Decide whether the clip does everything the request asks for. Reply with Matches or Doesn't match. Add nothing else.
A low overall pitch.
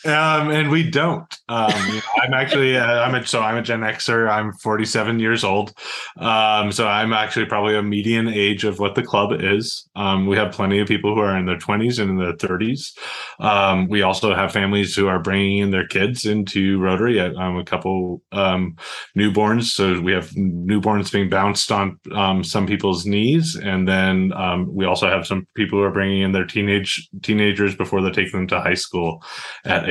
Matches